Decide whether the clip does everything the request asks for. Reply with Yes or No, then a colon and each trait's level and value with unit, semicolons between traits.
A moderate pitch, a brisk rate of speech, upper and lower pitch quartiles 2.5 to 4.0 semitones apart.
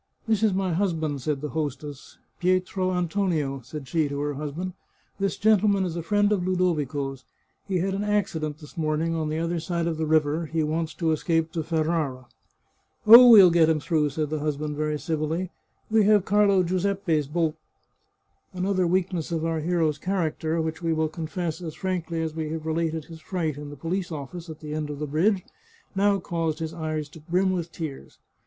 Yes: medium, 165 Hz; fast, 210 wpm; average, 3.1 semitones